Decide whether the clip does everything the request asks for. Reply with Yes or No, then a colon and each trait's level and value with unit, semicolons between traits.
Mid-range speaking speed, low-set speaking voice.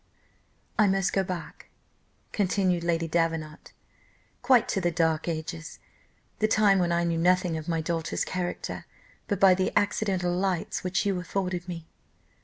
No: average, 150 wpm; medium, 180 Hz